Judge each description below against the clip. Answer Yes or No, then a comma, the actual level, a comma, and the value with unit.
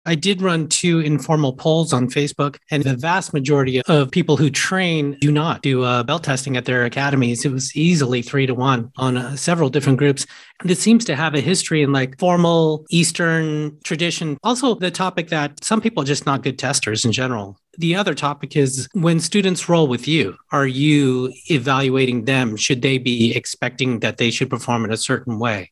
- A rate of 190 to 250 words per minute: Yes, average, 200 wpm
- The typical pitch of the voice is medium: Yes, medium, 145 Hz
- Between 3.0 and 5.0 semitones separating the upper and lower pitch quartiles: Yes, average, 4.2 semitones